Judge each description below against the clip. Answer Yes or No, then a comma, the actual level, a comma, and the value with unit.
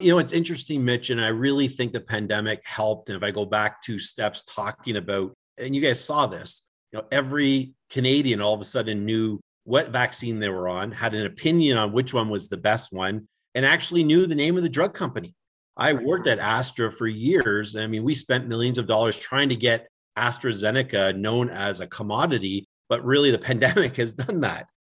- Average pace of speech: No, fast, 210 wpm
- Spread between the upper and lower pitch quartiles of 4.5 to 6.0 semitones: No, average, 4.0 semitones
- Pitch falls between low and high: No, low, 115 Hz